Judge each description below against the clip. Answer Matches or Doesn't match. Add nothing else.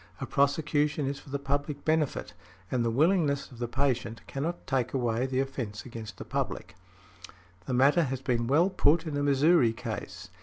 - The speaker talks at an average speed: Matches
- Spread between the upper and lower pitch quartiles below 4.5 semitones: Matches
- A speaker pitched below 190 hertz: Matches